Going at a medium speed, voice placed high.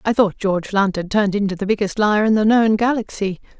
No: fast, 235 wpm; high, 205 Hz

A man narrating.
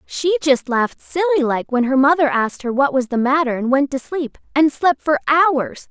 No: female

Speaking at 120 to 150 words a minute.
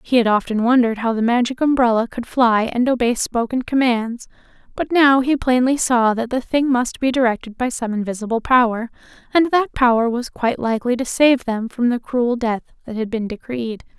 No: average, 195 wpm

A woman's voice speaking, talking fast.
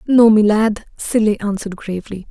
No: female; average, 155 wpm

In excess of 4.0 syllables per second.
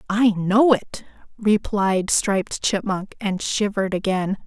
No: 3.9 syllables/s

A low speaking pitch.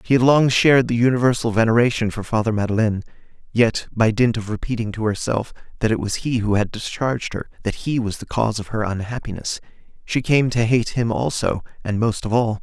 Yes: low, 115 Hz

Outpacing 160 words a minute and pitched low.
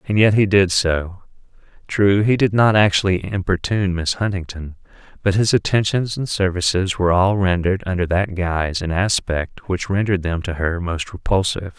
Yes: average, 170 wpm; very low, 95 Hz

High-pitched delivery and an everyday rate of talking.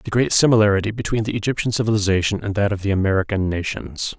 No: low, 105 Hz; average, 185 wpm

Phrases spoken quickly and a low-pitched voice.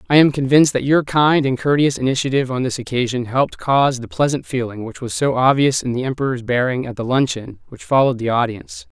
Yes: fast, 215 wpm; low, 130 Hz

